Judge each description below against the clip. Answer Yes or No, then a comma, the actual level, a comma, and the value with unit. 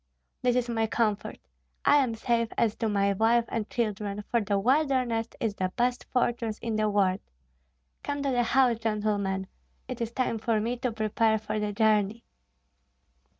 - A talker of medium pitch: No, high, 225 Hz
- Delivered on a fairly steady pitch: Yes, narrow, 2.3 semitones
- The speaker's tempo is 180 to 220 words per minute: No, average, 170 wpm